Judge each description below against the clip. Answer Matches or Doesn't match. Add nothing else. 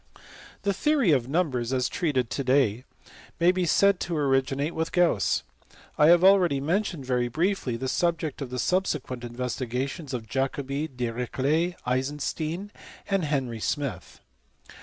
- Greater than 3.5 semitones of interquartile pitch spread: Matches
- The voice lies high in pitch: Doesn't match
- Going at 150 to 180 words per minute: Doesn't match